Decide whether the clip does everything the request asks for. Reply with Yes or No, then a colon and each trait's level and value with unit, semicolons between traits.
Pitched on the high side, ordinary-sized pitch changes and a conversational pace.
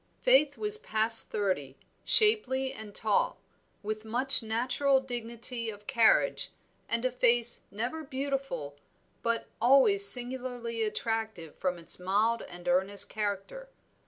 No: high, 230 Hz; average, 3.9 semitones; slow, 120 wpm